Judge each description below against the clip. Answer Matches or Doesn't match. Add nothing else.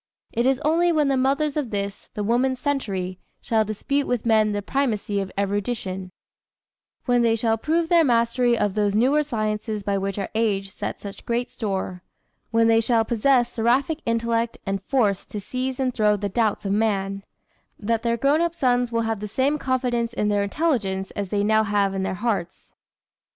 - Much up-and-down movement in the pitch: Doesn't match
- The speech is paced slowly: Doesn't match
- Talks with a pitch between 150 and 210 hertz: Doesn't match